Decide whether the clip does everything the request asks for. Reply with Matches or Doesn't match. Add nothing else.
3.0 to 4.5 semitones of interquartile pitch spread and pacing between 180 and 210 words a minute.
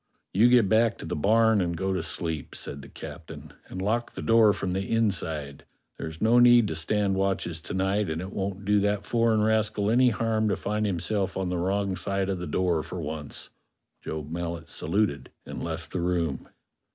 Matches